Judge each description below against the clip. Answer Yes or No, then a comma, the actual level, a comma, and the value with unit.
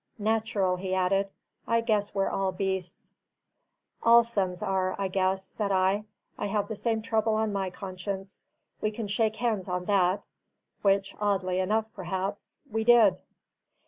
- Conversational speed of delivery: Yes, average, 150 wpm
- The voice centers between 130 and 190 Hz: No, high, 200 Hz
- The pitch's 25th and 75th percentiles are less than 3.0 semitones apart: Yes, narrow, 2.4 semitones